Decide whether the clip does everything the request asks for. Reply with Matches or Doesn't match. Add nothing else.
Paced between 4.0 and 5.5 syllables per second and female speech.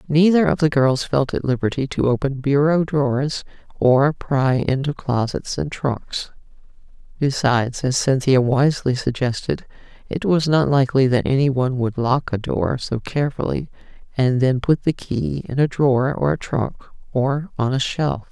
Matches